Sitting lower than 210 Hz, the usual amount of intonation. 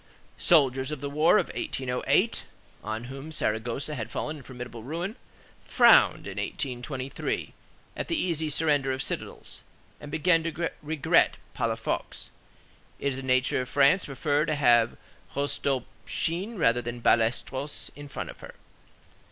Yes: medium, 140 Hz; average, 3.5 semitones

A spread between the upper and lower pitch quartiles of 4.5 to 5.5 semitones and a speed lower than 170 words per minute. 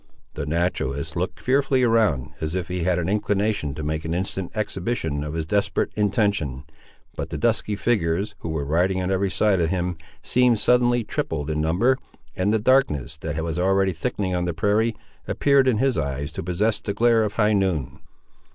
No: average, 5.0 semitones; average, 190 wpm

